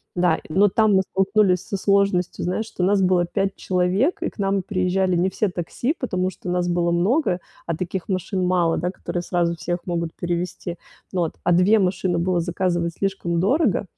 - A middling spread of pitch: No, narrow, 1.9 semitones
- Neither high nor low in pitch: Yes, medium, 180 Hz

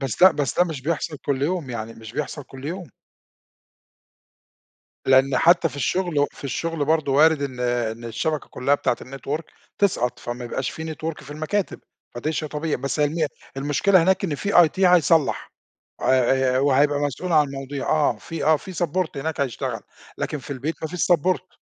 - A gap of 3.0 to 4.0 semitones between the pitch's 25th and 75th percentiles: Yes, average, 3.6 semitones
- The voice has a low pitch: No, medium, 145 Hz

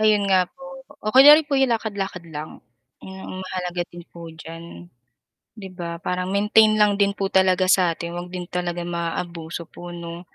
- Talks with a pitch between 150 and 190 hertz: Yes, medium, 185 Hz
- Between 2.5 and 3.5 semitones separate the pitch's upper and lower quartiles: Yes, average, 3.1 semitones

